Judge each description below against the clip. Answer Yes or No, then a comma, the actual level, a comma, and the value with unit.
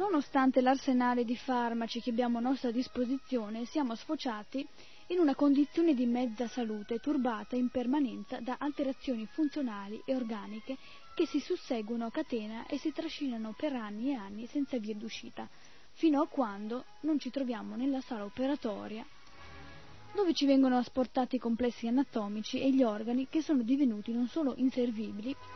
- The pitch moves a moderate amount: Yes, average, 3.1 semitones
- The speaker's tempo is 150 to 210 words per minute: Yes, average, 155 wpm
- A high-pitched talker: Yes, very high, 255 Hz